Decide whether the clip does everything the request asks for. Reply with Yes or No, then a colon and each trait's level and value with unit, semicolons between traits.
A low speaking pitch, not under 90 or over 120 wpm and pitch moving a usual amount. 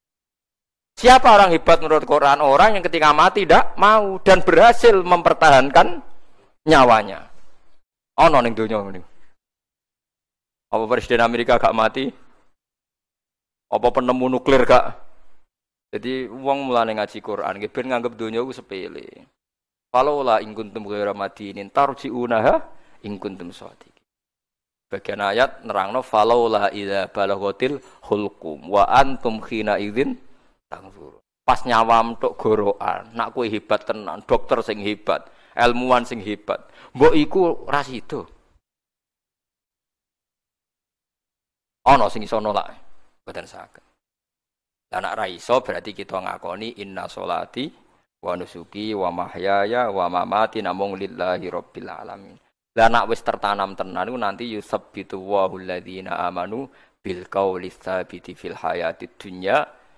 Yes: low, 115 Hz; average, 110 wpm; average, 4.8 semitones